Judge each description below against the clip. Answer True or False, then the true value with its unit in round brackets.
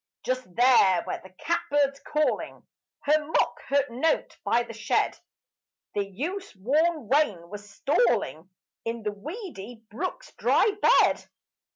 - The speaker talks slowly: True (130 wpm)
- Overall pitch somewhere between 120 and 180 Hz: False (245 Hz)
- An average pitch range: False (6.7 semitones)